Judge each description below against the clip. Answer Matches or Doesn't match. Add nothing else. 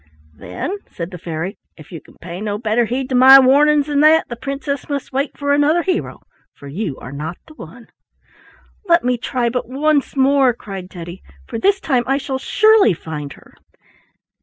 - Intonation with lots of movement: Matches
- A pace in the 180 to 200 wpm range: Matches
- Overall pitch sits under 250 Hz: Doesn't match